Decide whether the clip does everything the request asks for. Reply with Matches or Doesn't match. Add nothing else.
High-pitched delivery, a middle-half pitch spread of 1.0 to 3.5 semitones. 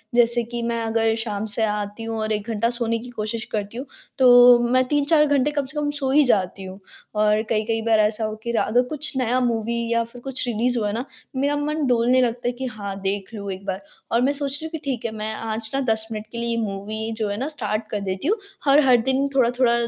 Matches